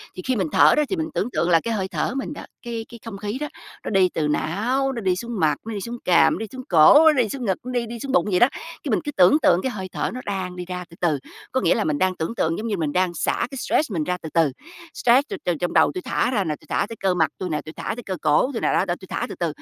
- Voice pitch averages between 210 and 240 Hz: No, high, 200 Hz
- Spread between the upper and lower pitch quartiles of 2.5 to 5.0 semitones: No, wide, 5.5 semitones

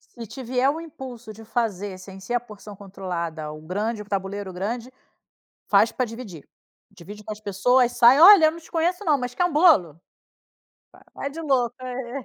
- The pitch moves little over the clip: No, average, 5.1 semitones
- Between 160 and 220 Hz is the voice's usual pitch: No, high, 230 Hz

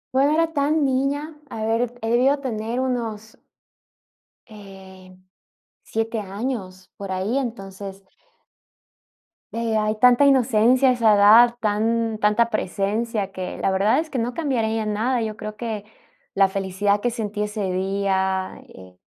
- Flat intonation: No, average, 3.6 semitones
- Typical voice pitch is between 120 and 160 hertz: No, high, 220 Hz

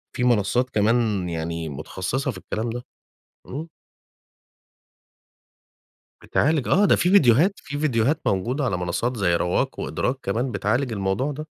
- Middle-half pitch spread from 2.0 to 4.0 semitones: No, wide, 5.6 semitones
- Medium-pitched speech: No, low, 120 Hz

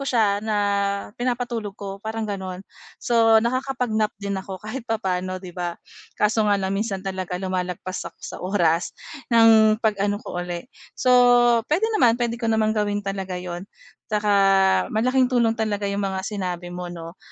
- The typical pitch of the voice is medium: No, high, 205 Hz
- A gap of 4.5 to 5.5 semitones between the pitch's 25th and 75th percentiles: No, average, 3.3 semitones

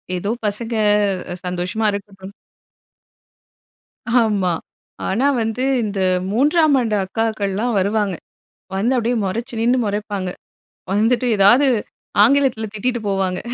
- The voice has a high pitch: Yes, high, 215 Hz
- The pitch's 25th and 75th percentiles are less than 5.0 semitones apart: Yes, average, 3.3 semitones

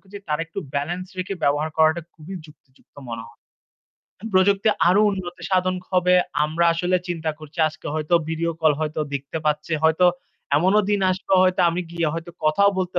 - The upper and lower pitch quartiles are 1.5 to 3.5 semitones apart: Yes, average, 3.1 semitones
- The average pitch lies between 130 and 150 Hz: No, medium, 170 Hz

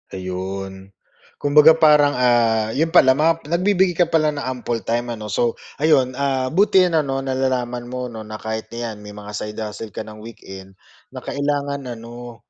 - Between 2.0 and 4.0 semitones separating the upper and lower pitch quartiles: No, average, 4.9 semitones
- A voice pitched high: No, low, 125 Hz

